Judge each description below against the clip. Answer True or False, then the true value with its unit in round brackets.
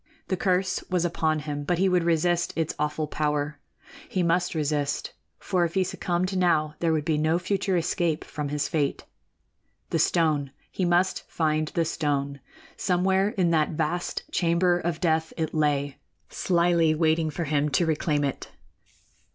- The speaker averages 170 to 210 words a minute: False (160 wpm)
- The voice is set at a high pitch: False (165 Hz)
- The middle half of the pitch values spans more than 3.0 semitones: False (2.6 semitones)